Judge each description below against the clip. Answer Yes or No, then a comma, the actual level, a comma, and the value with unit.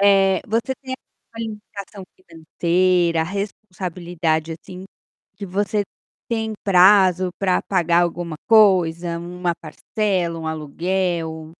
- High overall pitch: No, medium, 180 Hz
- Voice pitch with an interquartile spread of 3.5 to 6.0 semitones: No, average, 2.9 semitones